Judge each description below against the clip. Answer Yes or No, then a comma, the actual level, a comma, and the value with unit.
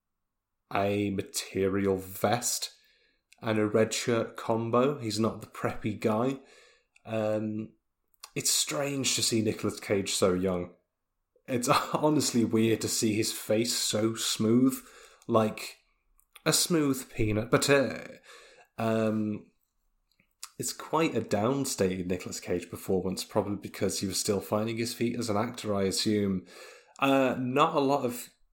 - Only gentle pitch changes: No, average, 3.5 semitones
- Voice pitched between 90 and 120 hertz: Yes, low, 110 Hz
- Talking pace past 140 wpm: No, slow, 135 wpm